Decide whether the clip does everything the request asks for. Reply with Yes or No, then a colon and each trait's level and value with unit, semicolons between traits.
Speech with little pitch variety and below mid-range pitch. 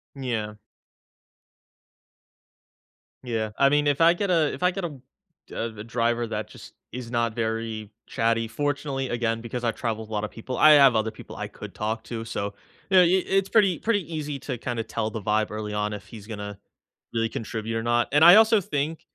No: average, 4.9 semitones; low, 115 Hz